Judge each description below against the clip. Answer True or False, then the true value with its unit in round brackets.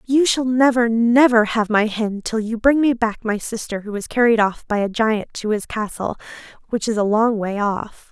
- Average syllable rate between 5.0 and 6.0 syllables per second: False (4.7 syllables/s)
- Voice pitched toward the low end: False (225 Hz)